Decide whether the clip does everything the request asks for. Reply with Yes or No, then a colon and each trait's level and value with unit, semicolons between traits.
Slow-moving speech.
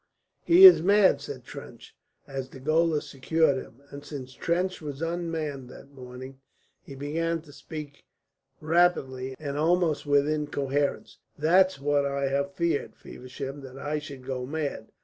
No: average, 150 wpm